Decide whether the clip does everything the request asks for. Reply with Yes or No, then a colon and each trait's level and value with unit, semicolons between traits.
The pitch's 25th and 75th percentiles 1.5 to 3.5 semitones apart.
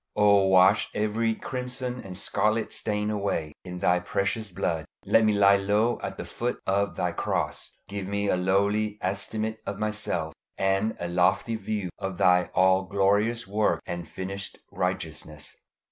Yes: narrow, 2.6 semitones